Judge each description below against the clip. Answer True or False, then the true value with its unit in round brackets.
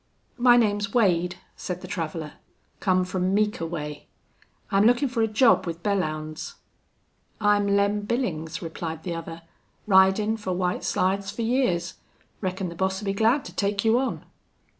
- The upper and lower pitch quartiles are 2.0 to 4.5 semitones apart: True (3.7 semitones)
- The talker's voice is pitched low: False (195 Hz)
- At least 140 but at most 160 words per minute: True (155 wpm)